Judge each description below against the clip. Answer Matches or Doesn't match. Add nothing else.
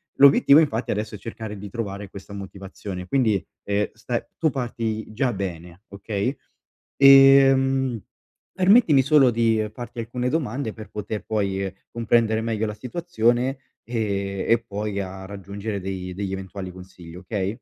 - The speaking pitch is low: Matches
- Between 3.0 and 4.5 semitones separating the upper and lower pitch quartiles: Matches